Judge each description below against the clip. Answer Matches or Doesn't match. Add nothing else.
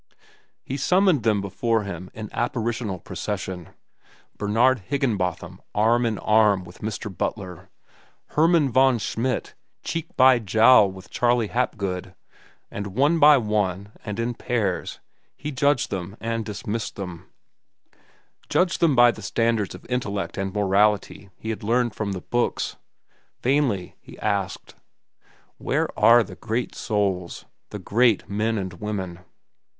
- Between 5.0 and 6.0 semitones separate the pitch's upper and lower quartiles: Doesn't match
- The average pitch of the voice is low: Matches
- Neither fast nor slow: Doesn't match